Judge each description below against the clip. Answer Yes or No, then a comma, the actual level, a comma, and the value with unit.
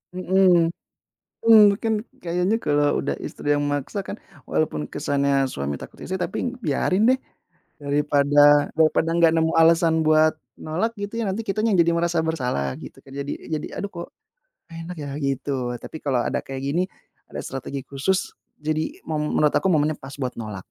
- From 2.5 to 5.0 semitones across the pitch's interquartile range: Yes, average, 4.0 semitones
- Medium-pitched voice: Yes, medium, 155 Hz